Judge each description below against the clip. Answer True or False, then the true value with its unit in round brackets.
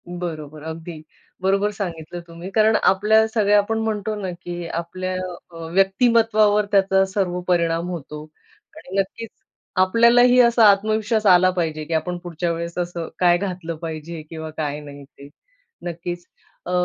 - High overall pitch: False (180 Hz)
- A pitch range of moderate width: True (3.7 semitones)